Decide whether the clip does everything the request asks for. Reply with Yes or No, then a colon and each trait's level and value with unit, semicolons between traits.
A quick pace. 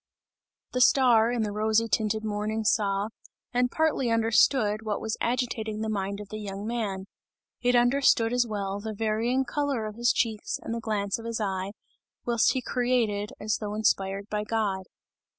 No: average, 170 wpm